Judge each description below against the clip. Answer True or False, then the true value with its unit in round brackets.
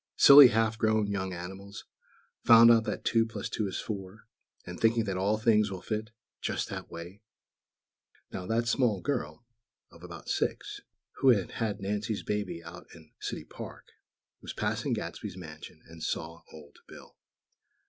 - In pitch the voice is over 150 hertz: False (105 Hz)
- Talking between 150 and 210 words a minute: True (160 wpm)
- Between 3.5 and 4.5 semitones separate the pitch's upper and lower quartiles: True (4.0 semitones)